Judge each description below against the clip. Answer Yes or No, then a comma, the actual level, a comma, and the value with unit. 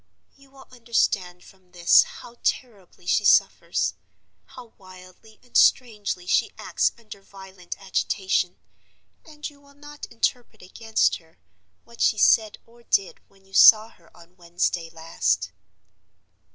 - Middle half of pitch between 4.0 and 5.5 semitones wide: Yes, average, 4.5 semitones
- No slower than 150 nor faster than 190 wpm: No, slow, 135 wpm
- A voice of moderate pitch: No, high, 200 Hz